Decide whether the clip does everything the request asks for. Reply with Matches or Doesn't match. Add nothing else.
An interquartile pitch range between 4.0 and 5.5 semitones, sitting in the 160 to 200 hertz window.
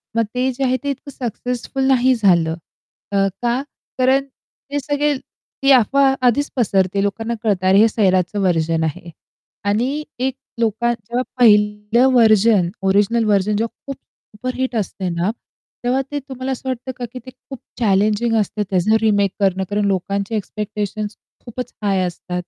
Doesn't match